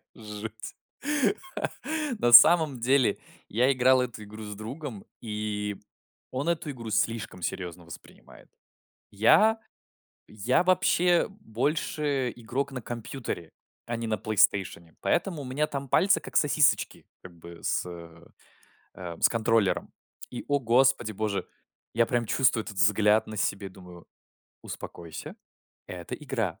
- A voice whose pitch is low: Yes, low, 115 Hz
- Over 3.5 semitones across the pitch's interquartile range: Yes, average, 4.7 semitones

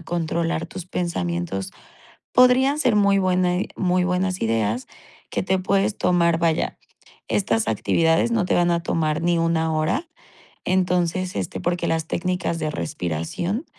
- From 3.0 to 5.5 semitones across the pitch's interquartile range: No, narrow, 2.4 semitones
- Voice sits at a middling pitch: Yes, medium, 175 Hz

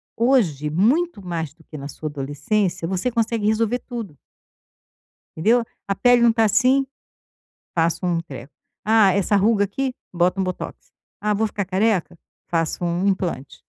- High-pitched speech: Yes, high, 195 Hz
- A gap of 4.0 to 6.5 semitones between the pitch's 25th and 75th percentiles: Yes, average, 5.2 semitones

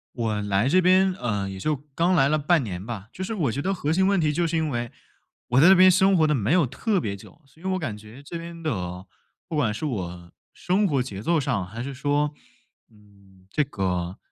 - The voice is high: No, medium, 140 Hz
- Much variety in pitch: Yes, wide, 8.4 semitones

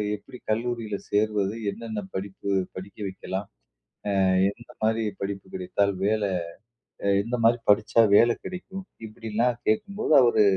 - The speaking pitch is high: No, low, 110 Hz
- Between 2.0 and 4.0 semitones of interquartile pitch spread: Yes, average, 3.0 semitones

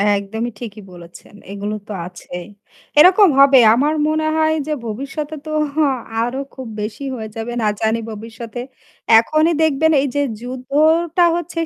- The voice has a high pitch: Yes, very high, 255 Hz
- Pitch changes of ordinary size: No, wide, 6.1 semitones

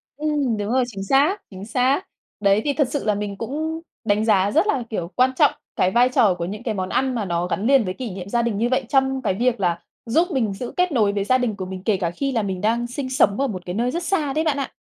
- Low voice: No, high, 235 Hz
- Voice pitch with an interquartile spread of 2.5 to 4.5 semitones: No, average, 5.2 semitones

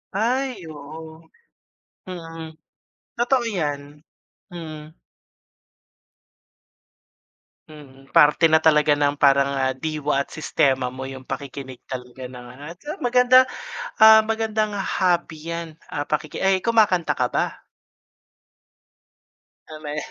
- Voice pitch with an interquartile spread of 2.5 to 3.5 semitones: No, average, 5.1 semitones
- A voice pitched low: No, medium, 155 Hz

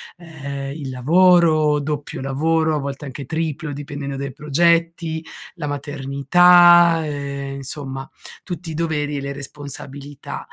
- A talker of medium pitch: Yes, medium, 145 Hz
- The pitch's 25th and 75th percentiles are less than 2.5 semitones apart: No, average, 2.8 semitones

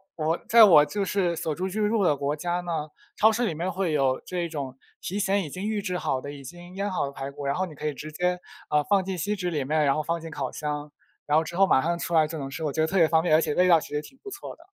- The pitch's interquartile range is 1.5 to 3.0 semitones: No, average, 3.9 semitones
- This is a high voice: No, medium, 165 Hz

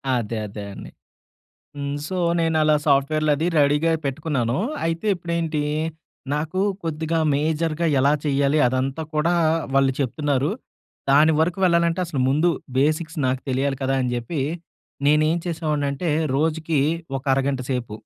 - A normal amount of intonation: Yes, average, 3.0 semitones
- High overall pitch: No, medium, 150 Hz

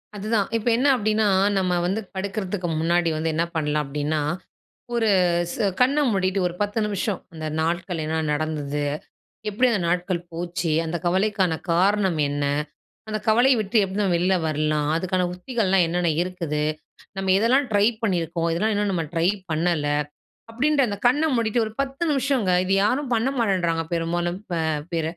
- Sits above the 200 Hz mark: No, medium, 185 Hz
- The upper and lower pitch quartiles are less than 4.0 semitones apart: No, average, 4.4 semitones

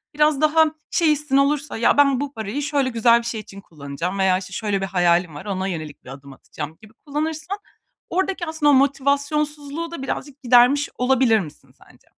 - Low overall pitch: No, very high, 260 Hz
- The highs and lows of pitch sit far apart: Yes, wide, 7.2 semitones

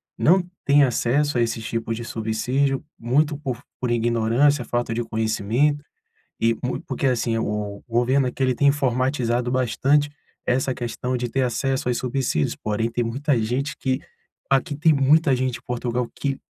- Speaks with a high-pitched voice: No, low, 125 Hz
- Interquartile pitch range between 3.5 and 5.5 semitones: No, average, 2.8 semitones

